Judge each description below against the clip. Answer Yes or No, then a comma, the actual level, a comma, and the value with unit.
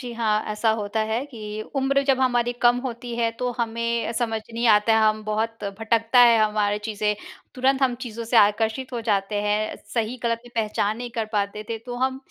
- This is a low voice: No, high, 230 Hz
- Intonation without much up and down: Yes, narrow, 2.2 semitones